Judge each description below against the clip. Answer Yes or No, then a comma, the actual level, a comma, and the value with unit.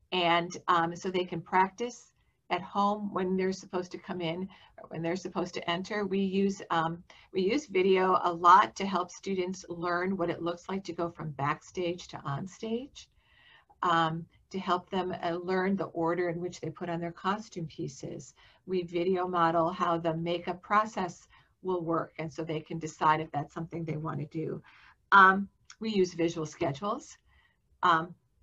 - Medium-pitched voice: Yes, medium, 175 Hz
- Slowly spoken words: No, average, 180 wpm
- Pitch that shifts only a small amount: Yes, narrow, 2.2 semitones